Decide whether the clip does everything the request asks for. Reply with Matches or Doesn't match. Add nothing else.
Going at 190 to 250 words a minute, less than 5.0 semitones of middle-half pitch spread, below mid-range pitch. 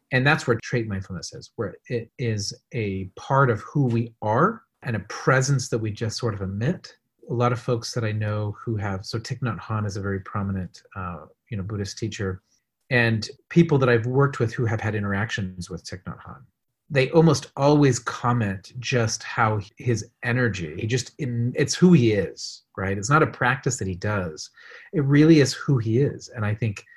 Matches